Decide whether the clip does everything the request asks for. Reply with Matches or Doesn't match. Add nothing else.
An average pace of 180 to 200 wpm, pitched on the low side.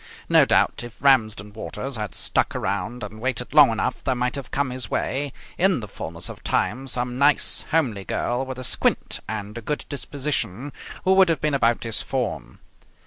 Matches